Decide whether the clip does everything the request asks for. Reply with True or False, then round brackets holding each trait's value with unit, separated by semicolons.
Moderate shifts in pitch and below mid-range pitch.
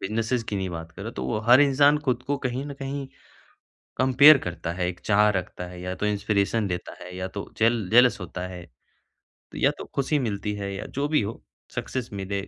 False (5.7 semitones; 105 Hz)